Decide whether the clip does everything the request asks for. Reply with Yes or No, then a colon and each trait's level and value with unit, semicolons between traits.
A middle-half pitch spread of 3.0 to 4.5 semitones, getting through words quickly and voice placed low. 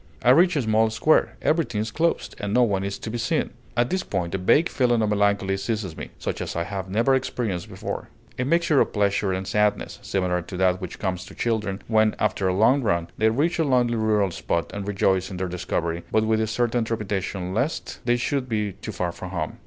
Yes: average, 4.1 semitones; fast, 225 wpm; low, 105 Hz